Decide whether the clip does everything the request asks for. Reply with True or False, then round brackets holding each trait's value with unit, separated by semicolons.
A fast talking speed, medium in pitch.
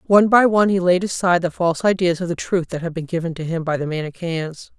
True (265 wpm; 175 Hz)